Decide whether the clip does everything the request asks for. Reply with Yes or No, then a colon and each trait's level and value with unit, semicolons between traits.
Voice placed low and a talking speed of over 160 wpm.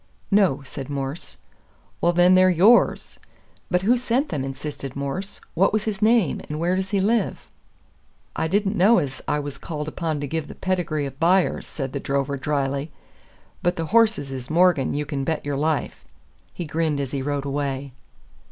No: medium, 155 Hz; average, 180 wpm